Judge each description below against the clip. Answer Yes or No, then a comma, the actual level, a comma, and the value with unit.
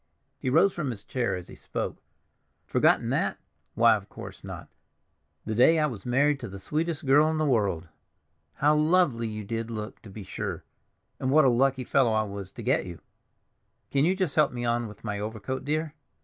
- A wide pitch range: Yes, wide, 5.7 semitones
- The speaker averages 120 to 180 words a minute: No, average, 200 wpm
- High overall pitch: No, low, 125 Hz